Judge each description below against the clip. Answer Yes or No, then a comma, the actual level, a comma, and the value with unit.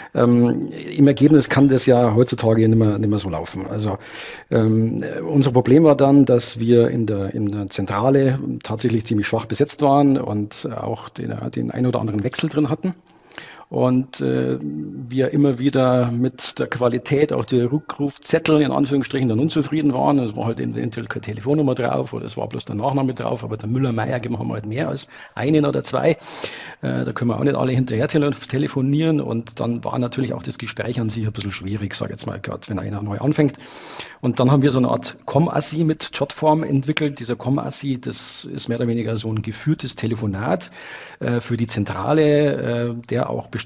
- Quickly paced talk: Yes, fast, 195 wpm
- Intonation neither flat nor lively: Yes, average, 4.2 semitones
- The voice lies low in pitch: Yes, low, 125 Hz